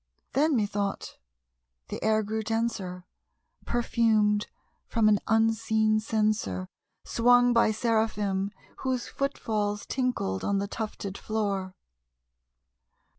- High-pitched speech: Yes, high, 215 Hz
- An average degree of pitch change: No, narrow, 2.1 semitones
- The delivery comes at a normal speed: No, slow, 100 wpm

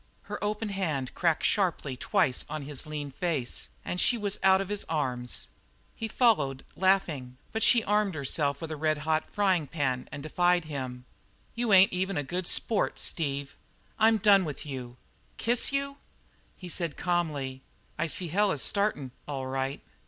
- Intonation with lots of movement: Yes, wide, 5.9 semitones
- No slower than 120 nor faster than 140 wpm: No, average, 170 wpm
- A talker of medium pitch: Yes, medium, 165 Hz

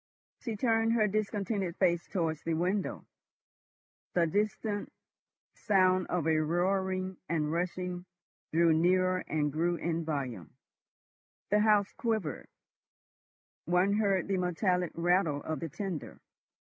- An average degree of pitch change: Yes, average, 3.3 semitones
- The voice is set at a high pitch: No, medium, 180 Hz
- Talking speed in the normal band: No, slow, 120 wpm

